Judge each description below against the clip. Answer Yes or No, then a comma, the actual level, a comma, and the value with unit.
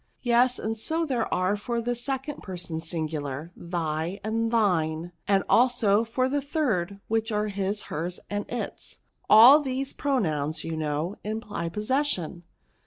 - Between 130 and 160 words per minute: Yes, average, 150 wpm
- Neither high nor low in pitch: No, high, 210 Hz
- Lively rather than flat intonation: Yes, wide, 6.1 semitones